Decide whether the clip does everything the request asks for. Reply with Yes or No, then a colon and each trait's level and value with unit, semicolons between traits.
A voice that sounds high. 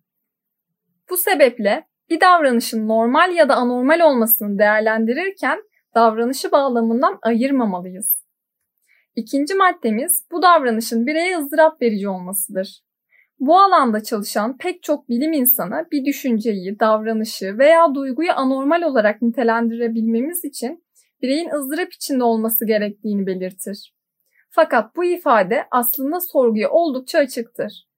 Yes: high, 245 Hz